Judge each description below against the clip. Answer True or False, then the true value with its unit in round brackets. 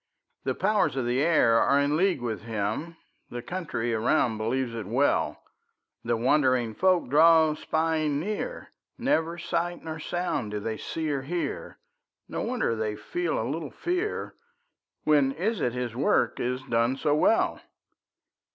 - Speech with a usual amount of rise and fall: False (5.9 semitones)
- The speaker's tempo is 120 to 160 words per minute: True (150 wpm)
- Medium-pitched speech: True (145 Hz)